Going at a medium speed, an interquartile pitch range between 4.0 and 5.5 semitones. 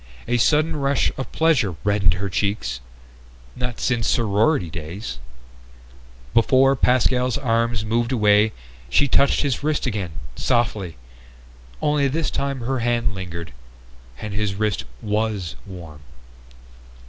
No: slow, 120 wpm; average, 4.6 semitones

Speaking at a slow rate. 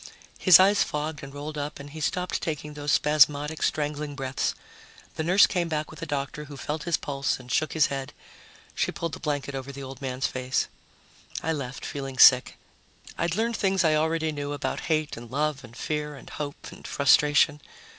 No: average, 195 wpm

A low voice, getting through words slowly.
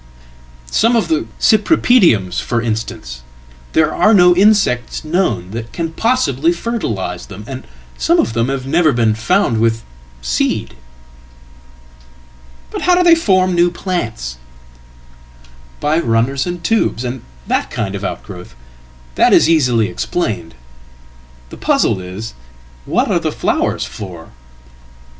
Yes: low, 115 Hz; slow, 115 wpm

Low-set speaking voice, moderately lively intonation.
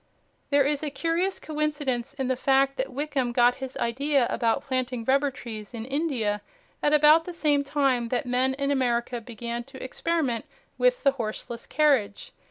No: very high, 265 Hz; average, 3.4 semitones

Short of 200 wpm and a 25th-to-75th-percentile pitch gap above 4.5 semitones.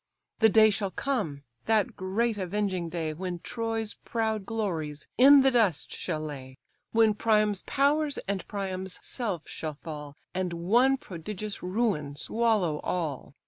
Yes: average, 140 wpm; average, 5.2 semitones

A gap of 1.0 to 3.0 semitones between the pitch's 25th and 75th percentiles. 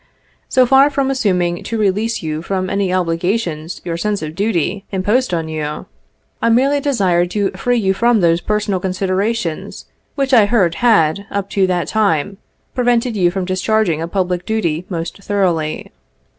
No: average, 4.3 semitones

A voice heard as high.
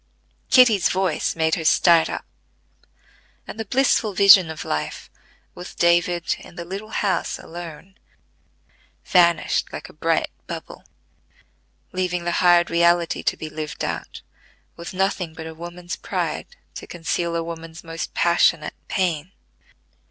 No: medium, 175 Hz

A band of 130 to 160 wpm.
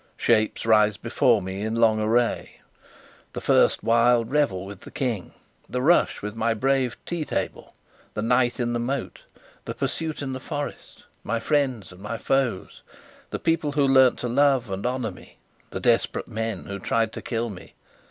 No: average, 175 wpm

